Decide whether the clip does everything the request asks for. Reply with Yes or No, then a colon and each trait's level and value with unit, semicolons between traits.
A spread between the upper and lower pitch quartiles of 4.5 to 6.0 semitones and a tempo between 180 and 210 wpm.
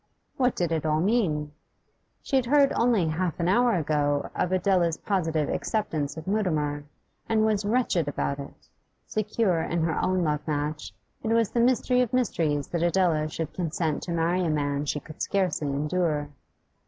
No: wide, 5.5 semitones; average, 170 wpm